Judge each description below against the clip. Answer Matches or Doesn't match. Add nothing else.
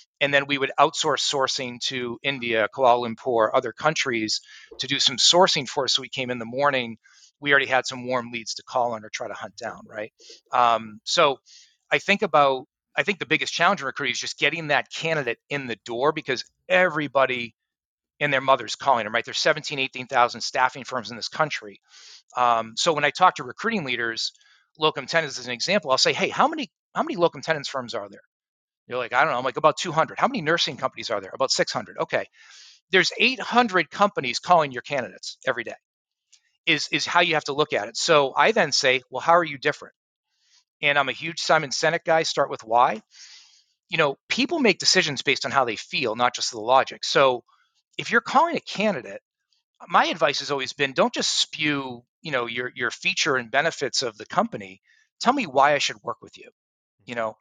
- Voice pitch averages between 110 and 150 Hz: Matches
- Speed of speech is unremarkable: Doesn't match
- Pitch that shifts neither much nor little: Matches